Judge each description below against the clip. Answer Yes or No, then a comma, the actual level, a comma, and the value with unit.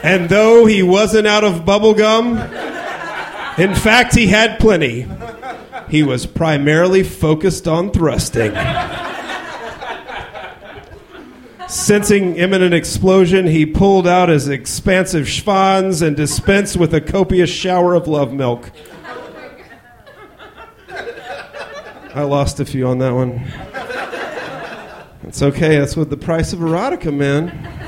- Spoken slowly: Yes, slow, 110 wpm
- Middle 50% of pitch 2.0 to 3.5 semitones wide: No, average, 4.7 semitones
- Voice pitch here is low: No, medium, 175 Hz